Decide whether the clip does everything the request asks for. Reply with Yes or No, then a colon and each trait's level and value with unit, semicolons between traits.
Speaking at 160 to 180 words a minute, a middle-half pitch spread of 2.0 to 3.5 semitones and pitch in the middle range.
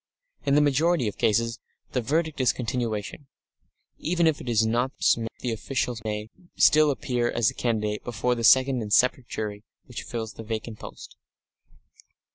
No: average, 165 wpm; average, 3.2 semitones; low, 120 Hz